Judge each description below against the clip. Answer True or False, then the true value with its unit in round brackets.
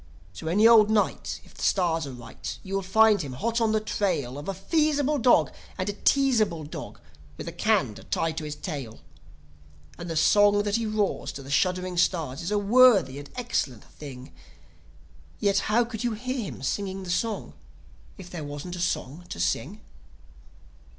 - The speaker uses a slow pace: False (185 wpm)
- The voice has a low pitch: False (190 Hz)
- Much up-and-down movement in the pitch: True (6.2 semitones)